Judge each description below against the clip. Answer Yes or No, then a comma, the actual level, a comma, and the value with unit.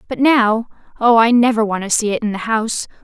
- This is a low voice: No, high, 225 Hz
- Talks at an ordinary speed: No, fast, 235 wpm